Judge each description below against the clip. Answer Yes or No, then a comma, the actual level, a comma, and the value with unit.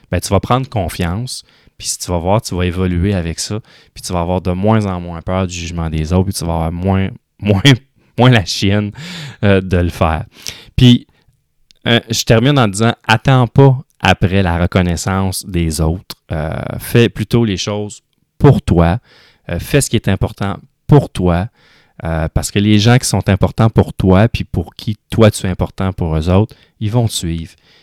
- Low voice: Yes, low, 100 Hz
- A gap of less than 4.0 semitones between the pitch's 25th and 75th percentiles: No, average, 4.3 semitones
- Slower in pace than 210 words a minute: Yes, average, 200 wpm